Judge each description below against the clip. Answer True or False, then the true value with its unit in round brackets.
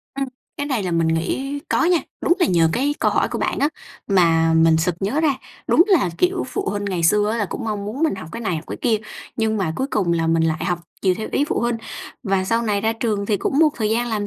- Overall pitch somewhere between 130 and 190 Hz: False (210 Hz)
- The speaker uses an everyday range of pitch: False (5.7 semitones)